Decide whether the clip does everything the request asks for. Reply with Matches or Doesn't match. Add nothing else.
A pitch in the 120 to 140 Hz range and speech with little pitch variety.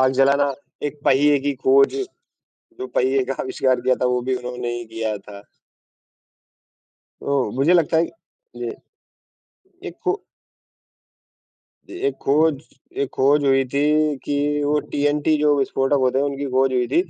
Matches